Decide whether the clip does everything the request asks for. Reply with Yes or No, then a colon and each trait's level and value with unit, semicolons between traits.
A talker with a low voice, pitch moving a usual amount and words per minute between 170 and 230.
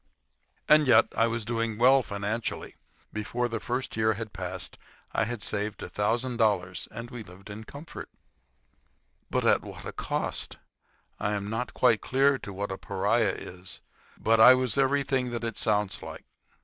Yes: low, 115 Hz; average, 3.1 semitones; average, 175 wpm